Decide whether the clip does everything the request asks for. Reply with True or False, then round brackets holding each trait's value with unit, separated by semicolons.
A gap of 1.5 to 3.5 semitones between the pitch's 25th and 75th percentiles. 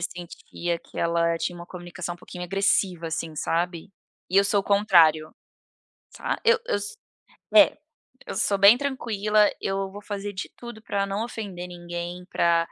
True (2.9 semitones)